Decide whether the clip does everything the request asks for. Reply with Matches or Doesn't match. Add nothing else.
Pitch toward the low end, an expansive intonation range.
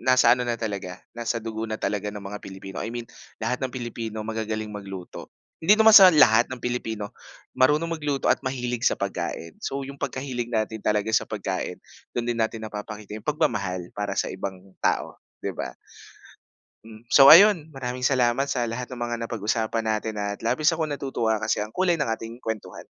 Doesn't match